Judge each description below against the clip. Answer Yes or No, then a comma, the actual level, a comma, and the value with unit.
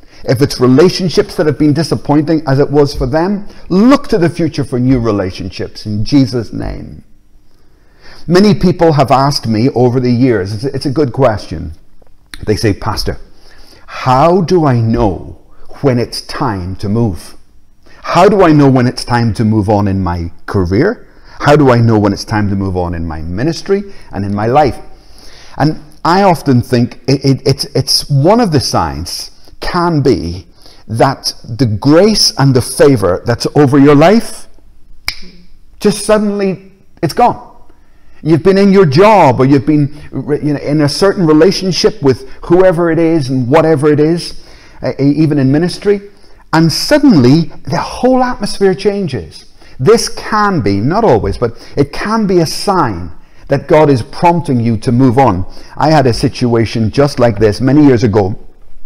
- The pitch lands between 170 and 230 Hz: No, medium, 140 Hz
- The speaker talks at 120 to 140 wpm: No, average, 165 wpm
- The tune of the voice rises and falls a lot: Yes, wide, 6.8 semitones